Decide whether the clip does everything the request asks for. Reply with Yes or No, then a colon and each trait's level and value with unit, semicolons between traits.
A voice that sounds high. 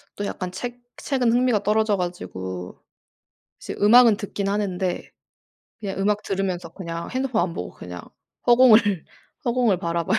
Yes: high, 200 Hz